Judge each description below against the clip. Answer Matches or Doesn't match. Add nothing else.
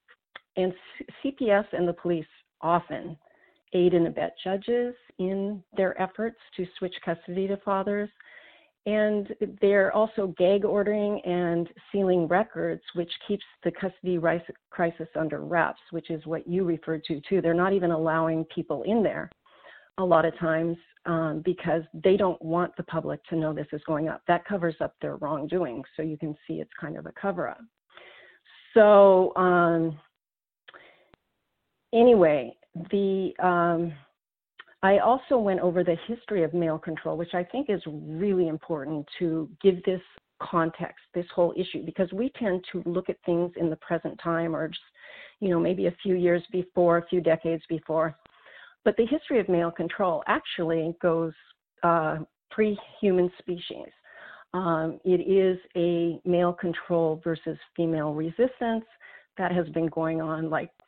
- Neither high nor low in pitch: Matches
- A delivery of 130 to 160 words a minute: Matches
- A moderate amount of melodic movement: Matches